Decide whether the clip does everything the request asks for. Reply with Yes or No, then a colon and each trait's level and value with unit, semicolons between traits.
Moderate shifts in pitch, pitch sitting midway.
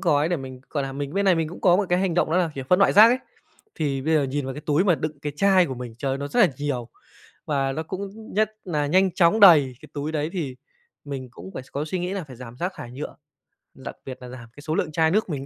Yes: average, 5.0 semitones; medium, 155 Hz